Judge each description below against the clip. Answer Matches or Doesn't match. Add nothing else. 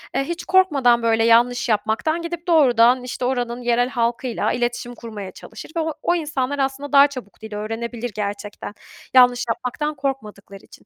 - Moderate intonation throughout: Matches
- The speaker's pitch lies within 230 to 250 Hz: Matches